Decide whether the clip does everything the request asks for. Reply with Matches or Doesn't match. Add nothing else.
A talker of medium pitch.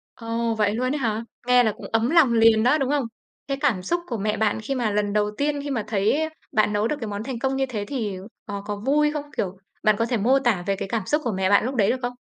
Doesn't match